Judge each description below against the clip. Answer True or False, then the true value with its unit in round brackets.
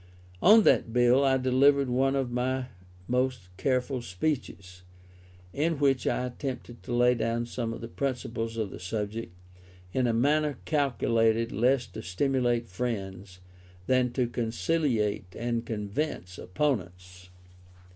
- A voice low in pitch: True (120 Hz)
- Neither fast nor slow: False (130 wpm)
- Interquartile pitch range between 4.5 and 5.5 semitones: False (3.3 semitones)